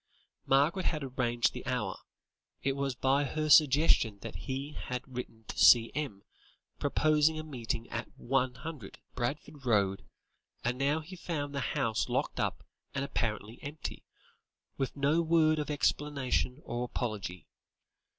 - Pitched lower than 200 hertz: Yes, low, 135 Hz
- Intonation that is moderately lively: Yes, average, 3.9 semitones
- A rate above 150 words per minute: No, slow, 135 wpm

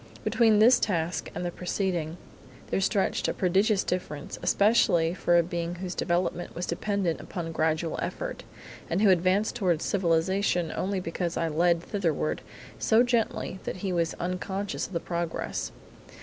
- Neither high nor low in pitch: Yes, medium, 180 Hz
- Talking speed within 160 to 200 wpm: No, average, 150 wpm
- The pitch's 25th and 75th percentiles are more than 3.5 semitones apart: No, average, 2.7 semitones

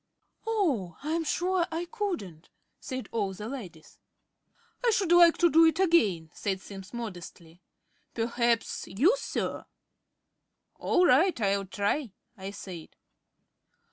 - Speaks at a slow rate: Yes, slow, 120 wpm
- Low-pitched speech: No, high, 235 Hz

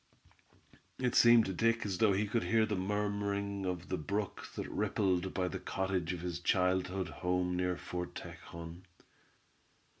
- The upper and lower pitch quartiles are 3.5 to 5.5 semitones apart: No, narrow, 2.4 semitones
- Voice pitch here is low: Yes, very low, 95 Hz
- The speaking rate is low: No, average, 155 wpm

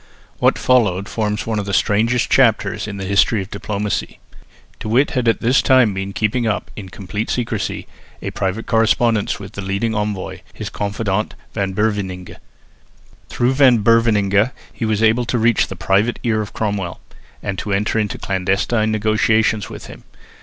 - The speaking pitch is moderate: No, low, 105 Hz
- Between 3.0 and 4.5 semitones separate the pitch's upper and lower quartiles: No, narrow, 2.4 semitones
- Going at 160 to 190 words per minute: Yes, average, 165 wpm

